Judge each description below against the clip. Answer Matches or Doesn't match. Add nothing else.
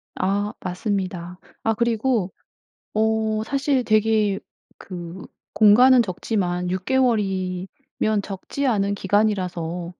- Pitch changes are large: Doesn't match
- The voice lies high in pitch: Matches